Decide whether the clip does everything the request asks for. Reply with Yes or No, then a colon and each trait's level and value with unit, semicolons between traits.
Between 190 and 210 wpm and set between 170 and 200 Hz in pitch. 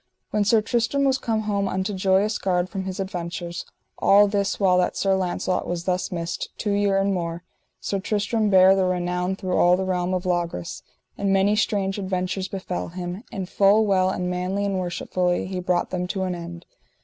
Yes: average, 195 wpm; high, 190 Hz